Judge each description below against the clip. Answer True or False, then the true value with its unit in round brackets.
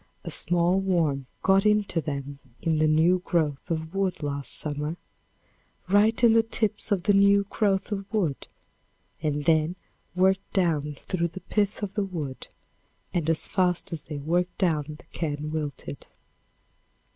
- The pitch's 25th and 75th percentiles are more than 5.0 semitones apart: False (4.3 semitones)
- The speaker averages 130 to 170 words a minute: True (155 wpm)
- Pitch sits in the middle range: True (170 Hz)